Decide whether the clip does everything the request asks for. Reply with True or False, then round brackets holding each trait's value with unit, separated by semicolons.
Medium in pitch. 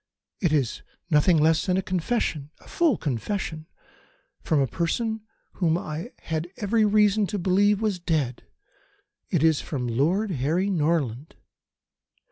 True (170 Hz)